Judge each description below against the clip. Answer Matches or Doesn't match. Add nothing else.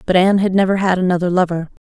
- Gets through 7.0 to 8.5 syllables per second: Matches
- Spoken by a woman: Matches